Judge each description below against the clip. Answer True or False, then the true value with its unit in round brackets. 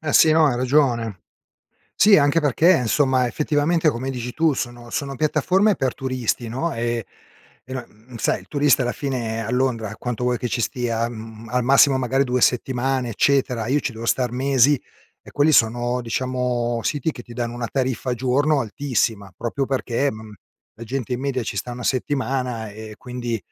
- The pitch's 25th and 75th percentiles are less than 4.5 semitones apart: True (2.7 semitones)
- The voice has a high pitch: False (125 Hz)